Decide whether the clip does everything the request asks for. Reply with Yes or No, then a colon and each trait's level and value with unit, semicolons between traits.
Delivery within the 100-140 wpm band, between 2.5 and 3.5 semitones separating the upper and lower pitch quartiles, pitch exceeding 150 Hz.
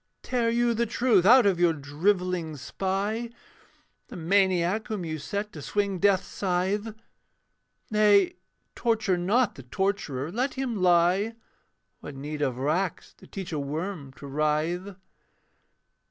No: slow, 135 wpm; average, 4.6 semitones; high, 190 Hz